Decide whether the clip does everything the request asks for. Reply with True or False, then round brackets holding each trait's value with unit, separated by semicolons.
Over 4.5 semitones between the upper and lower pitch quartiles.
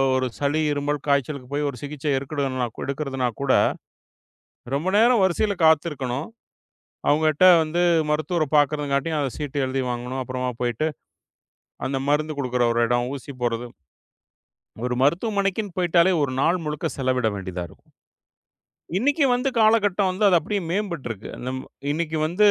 True (4.9 semitones)